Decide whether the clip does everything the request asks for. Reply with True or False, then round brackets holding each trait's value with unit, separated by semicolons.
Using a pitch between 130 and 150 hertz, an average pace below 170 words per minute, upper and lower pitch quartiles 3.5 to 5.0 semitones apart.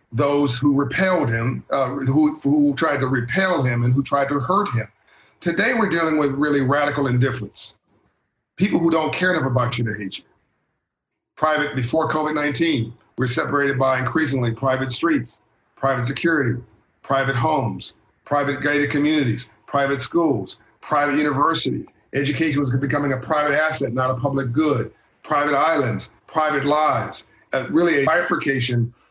False (140 Hz; 150 wpm; 2.8 semitones)